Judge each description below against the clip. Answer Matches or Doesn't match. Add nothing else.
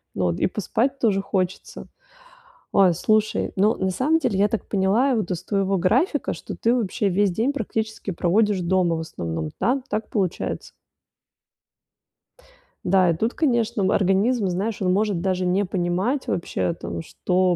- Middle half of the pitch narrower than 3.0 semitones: Doesn't match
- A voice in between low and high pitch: Doesn't match